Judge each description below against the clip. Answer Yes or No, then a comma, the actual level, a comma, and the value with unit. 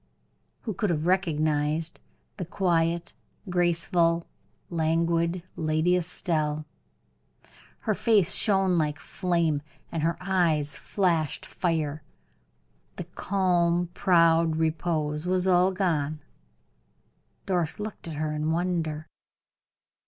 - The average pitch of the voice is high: No, medium, 170 Hz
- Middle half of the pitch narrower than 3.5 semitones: Yes, narrow, 2.4 semitones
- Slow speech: Yes, slow, 100 wpm